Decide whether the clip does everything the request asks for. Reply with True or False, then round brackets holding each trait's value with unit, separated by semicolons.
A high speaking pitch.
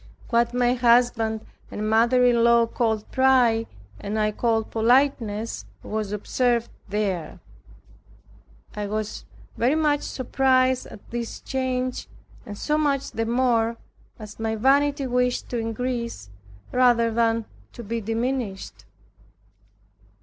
True (235 Hz)